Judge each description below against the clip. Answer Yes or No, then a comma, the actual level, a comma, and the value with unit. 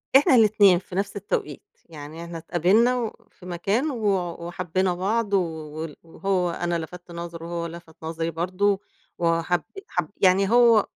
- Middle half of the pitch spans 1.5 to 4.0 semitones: Yes, average, 3.3 semitones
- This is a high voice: No, medium, 180 Hz